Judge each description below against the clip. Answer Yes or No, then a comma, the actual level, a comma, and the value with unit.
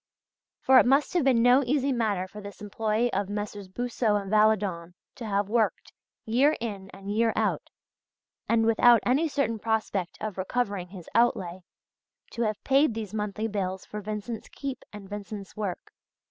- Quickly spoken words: No, average, 165 wpm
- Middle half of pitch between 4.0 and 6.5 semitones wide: No, average, 3.1 semitones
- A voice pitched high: Yes, high, 215 Hz